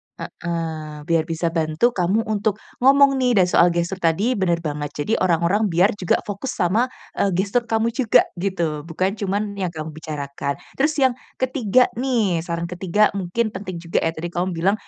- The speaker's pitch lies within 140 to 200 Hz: Yes, medium, 185 Hz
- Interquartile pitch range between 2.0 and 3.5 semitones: No, average, 4.6 semitones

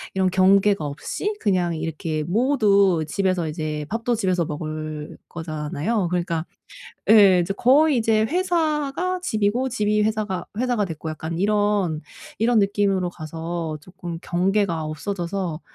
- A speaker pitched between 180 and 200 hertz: Yes, high, 190 Hz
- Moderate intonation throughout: Yes, average, 4.8 semitones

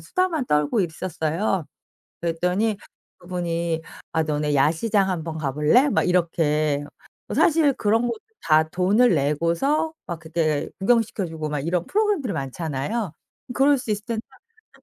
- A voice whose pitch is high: No, medium, 175 Hz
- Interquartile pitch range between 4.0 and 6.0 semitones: No, wide, 6.4 semitones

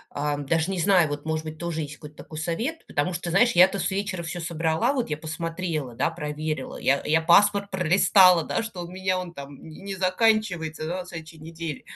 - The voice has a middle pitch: Yes, medium, 170 Hz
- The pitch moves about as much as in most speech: Yes, average, 3.1 semitones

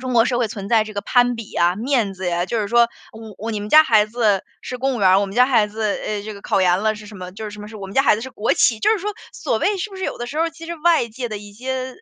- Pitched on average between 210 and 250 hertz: Yes, high, 220 Hz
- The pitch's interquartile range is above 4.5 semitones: No, average, 3.7 semitones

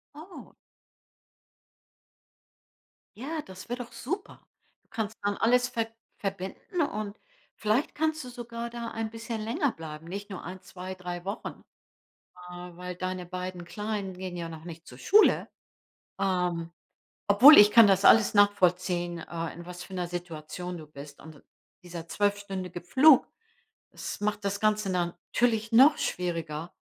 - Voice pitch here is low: No, high, 195 Hz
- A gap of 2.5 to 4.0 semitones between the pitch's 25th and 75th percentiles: No, average, 4.4 semitones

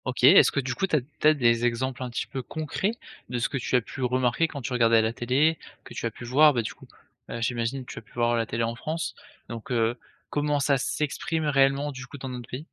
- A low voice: Yes, low, 130 Hz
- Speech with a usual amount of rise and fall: Yes, average, 3.6 semitones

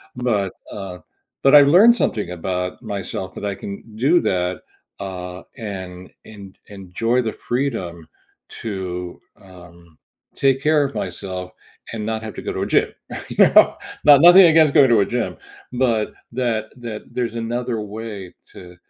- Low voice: Yes, low, 110 Hz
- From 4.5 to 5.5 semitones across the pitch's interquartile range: Yes, average, 5.1 semitones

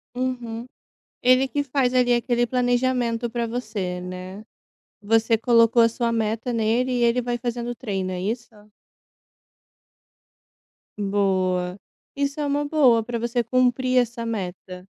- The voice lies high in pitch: Yes, high, 235 Hz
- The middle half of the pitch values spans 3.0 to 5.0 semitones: No, narrow, 2.6 semitones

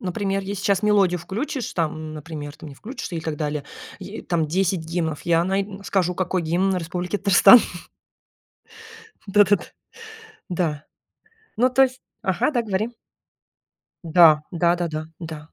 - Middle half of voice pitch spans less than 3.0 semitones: No, average, 3.7 semitones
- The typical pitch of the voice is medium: Yes, medium, 180 Hz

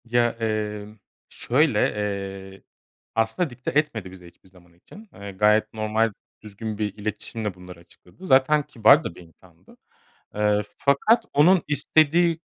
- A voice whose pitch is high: No, low, 110 Hz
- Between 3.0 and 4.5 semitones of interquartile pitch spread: No, wide, 5.4 semitones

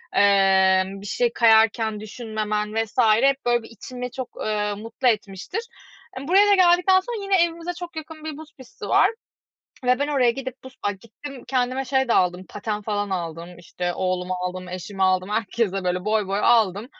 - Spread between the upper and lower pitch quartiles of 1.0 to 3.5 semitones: No, wide, 5.5 semitones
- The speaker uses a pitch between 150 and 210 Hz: No, high, 220 Hz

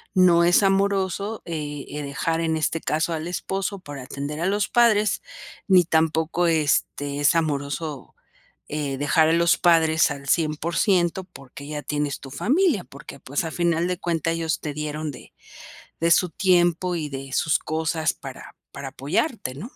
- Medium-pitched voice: Yes, medium, 160 Hz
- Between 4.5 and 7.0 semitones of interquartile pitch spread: No, average, 3.3 semitones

